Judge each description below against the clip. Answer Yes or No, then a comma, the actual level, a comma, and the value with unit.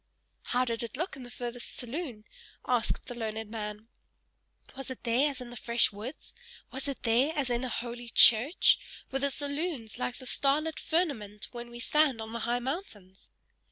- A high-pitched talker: Yes, high, 245 Hz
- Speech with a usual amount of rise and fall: Yes, average, 3.3 semitones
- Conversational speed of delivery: Yes, average, 185 wpm